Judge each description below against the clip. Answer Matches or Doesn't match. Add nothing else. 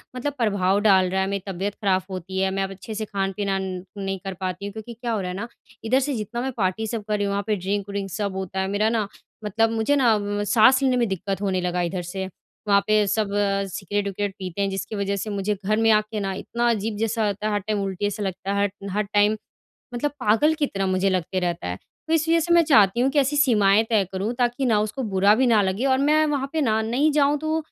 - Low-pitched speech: Doesn't match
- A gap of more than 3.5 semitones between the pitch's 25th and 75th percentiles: Doesn't match